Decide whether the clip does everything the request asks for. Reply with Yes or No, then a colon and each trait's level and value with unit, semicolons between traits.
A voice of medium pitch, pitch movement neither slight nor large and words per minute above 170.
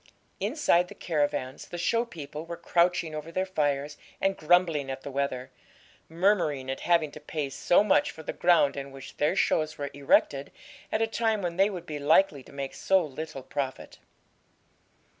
Yes: medium, 155 Hz; average, 4.0 semitones; average, 180 wpm